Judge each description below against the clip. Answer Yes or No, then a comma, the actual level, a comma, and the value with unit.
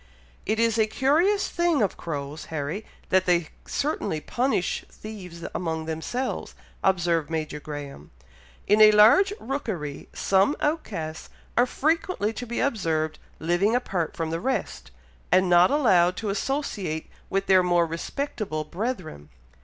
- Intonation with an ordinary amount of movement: No, wide, 6.8 semitones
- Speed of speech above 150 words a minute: No, slow, 135 wpm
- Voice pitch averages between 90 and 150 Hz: No, high, 190 Hz